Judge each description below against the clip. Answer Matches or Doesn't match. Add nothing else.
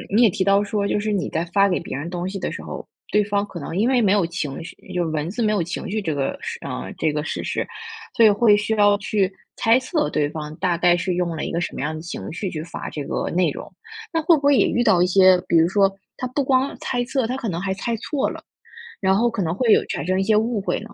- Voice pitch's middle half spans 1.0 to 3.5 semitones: Doesn't match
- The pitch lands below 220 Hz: Matches